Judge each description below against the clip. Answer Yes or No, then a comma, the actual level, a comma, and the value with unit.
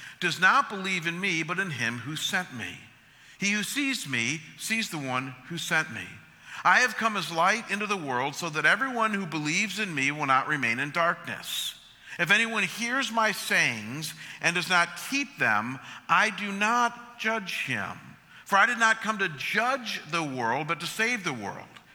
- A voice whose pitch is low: No, medium, 180 Hz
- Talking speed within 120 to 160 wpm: No, average, 190 wpm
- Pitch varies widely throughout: Yes, wide, 7.2 semitones